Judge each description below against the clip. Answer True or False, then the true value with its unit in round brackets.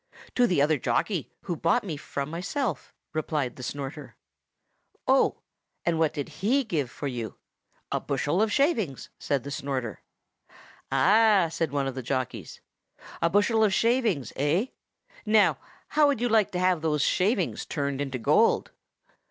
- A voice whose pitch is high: False (165 Hz)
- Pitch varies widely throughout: True (7.1 semitones)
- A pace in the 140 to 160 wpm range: True (155 wpm)